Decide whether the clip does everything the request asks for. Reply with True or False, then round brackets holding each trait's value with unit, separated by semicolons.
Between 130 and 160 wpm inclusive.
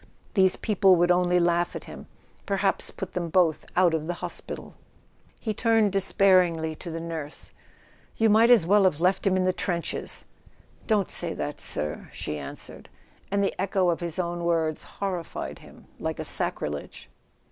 False (170 wpm)